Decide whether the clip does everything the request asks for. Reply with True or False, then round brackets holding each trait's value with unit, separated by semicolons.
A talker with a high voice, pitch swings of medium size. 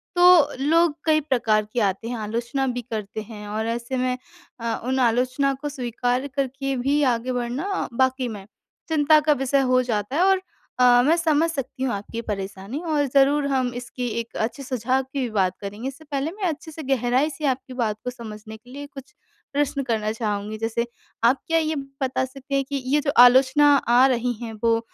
True (255 Hz; 3.3 semitones)